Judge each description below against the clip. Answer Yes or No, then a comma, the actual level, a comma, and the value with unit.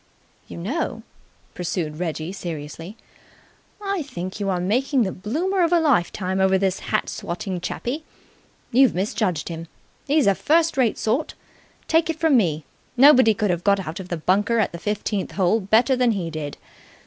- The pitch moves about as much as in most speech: No, wide, 6.7 semitones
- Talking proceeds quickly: No, average, 170 wpm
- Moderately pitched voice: No, high, 200 Hz